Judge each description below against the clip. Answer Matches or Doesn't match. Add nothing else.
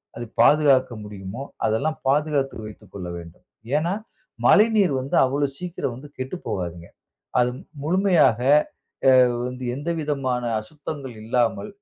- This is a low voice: Matches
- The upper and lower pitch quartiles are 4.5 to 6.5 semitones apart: Matches